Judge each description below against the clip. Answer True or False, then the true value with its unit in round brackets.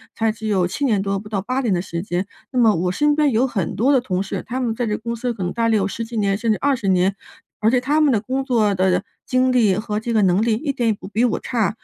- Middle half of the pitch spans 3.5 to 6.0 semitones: True (4.1 semitones)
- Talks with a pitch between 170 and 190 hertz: False (220 Hz)